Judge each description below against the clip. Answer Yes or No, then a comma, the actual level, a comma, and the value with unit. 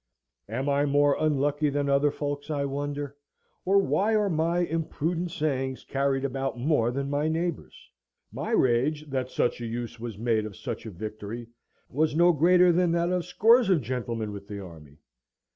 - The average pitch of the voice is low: No, medium, 145 Hz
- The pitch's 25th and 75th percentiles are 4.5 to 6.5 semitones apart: Yes, average, 5.2 semitones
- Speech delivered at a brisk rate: No, average, 175 wpm